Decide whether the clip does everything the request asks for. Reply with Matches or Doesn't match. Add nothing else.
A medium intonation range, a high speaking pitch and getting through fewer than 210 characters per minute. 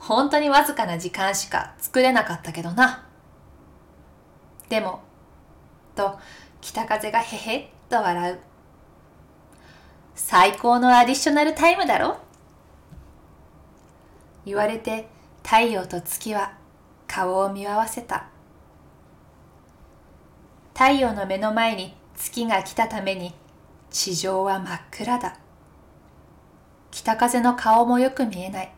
Doesn't match